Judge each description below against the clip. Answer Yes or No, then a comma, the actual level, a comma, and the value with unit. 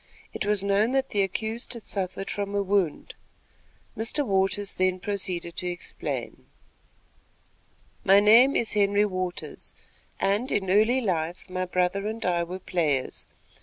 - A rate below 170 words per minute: Yes, average, 140 wpm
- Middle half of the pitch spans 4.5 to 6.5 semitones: No, narrow, 2.4 semitones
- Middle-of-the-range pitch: No, high, 195 Hz